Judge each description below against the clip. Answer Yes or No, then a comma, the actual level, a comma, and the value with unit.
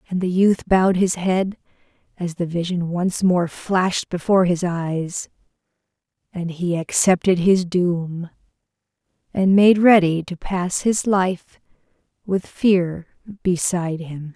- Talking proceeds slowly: Yes, slow, 130 wpm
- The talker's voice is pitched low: No, medium, 180 Hz